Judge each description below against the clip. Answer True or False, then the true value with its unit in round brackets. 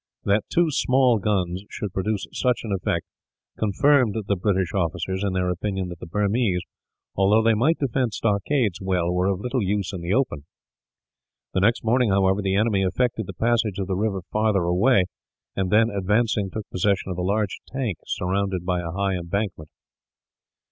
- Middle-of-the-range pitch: False (100 Hz)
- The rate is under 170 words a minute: False (175 wpm)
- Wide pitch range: False (3.1 semitones)